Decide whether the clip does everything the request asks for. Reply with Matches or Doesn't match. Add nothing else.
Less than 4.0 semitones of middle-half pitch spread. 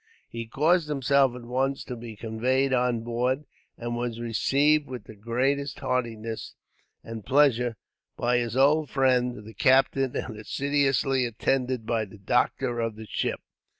Matches